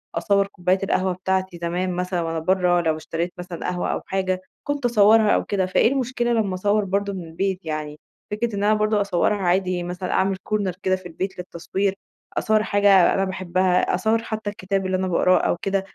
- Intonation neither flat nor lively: No, narrow, 2.1 semitones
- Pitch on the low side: No, high, 190 Hz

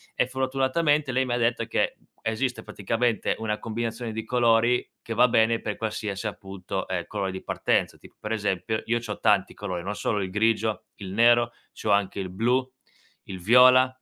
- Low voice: Yes, low, 110 Hz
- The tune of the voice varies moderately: Yes, average, 3.0 semitones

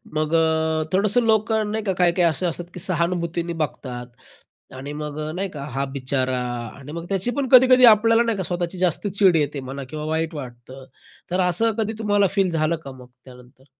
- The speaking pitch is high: No, medium, 170 Hz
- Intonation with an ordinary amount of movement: No, wide, 5.9 semitones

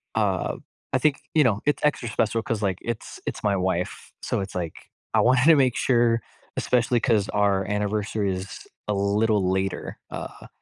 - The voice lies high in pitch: No, low, 105 Hz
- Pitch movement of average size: Yes, average, 3.4 semitones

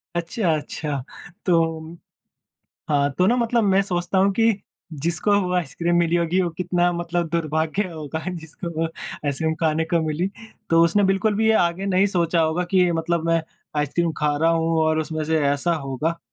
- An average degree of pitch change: No, narrow, 2.3 semitones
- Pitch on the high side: No, medium, 170 Hz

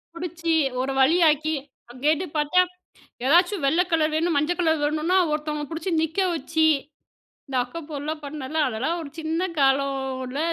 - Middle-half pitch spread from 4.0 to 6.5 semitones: No, average, 2.8 semitones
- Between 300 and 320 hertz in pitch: Yes, very high, 310 Hz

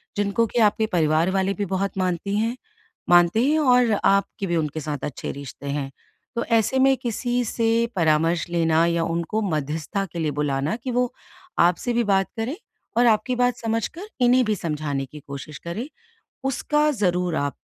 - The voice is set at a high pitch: Yes, high, 195 Hz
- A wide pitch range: Yes, wide, 6.8 semitones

